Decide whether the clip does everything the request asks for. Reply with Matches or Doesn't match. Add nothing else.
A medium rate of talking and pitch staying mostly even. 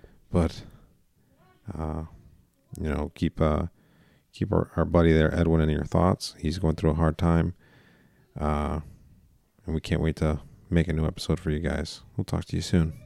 Matches